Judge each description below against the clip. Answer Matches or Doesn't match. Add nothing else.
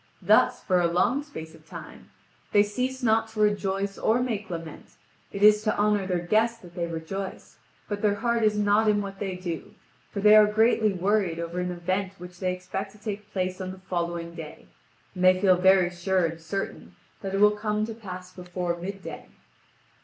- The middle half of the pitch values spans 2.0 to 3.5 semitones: Matches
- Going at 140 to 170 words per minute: Doesn't match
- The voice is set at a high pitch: Matches